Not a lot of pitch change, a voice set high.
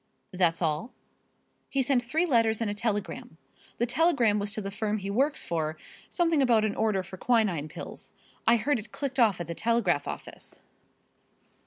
No: average, 4.4 semitones; high, 220 Hz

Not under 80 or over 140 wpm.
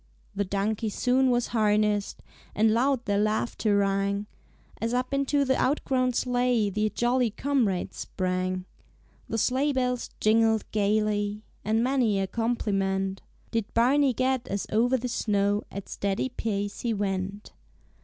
Yes: slow, 135 wpm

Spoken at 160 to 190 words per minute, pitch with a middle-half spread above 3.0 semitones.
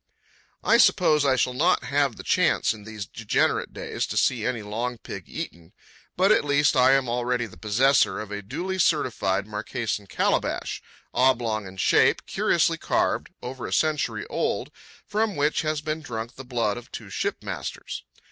Yes: average, 165 wpm; average, 5.2 semitones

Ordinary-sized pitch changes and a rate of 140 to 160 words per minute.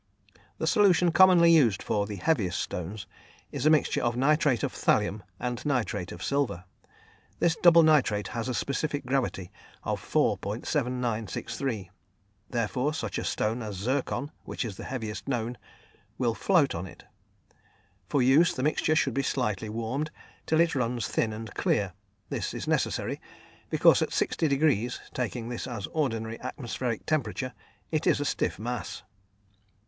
Yes: average, 4.7 semitones; average, 150 wpm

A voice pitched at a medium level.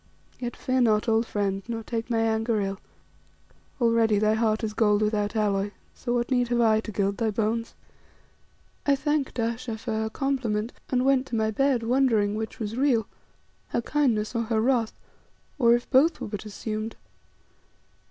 No: high, 225 Hz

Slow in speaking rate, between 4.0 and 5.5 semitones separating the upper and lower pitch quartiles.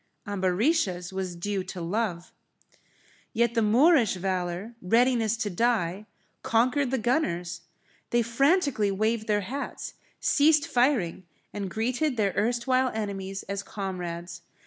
Yes: slow, 120 wpm; average, 4.5 semitones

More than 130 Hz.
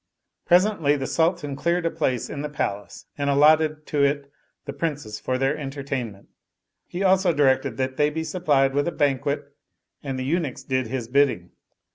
Yes: medium, 140 Hz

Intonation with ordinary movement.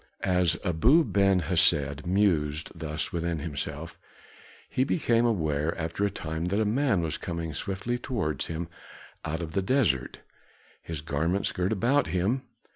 Yes: average, 4.4 semitones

